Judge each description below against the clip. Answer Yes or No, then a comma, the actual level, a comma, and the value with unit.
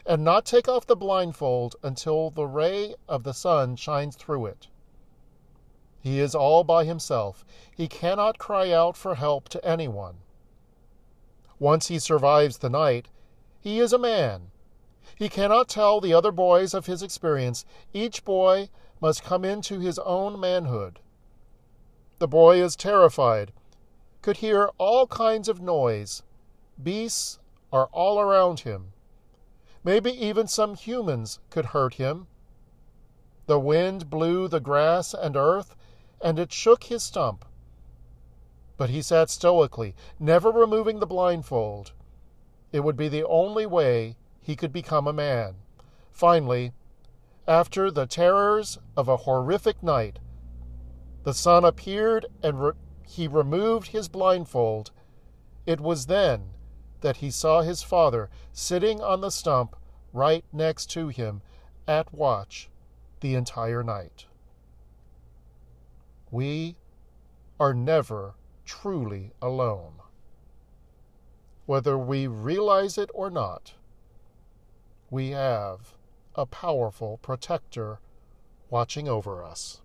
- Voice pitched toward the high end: No, medium, 140 Hz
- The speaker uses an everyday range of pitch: No, wide, 8.1 semitones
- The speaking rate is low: Yes, slow, 125 wpm